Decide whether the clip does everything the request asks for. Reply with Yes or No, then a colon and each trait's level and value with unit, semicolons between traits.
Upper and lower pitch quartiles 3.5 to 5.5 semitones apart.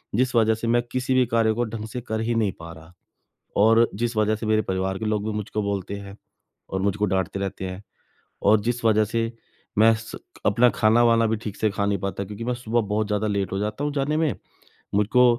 No: narrow, 2.4 semitones